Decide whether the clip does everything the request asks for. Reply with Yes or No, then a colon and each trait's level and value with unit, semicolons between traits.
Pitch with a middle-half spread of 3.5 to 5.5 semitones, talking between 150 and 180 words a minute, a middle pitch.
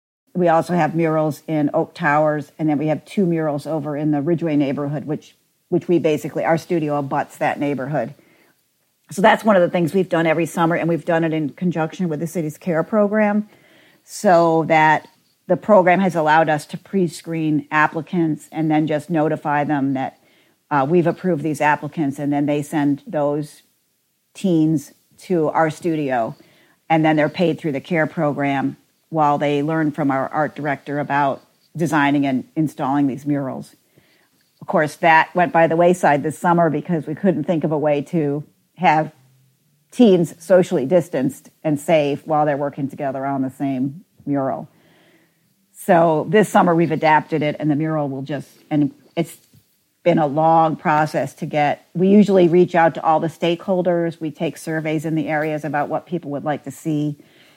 No: narrow, 2.4 semitones; average, 175 wpm; medium, 155 Hz